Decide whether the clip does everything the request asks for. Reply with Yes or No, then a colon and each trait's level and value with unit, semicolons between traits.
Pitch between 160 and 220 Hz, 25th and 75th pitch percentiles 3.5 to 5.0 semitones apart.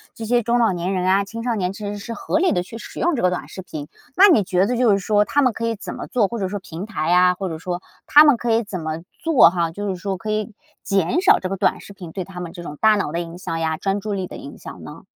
Yes: high, 195 Hz; average, 4.0 semitones